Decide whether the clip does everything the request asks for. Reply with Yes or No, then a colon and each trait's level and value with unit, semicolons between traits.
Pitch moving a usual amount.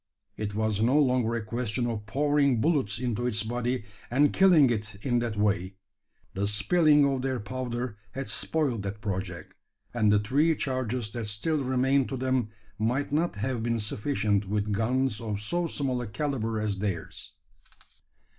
Yes: average, 4.0 semitones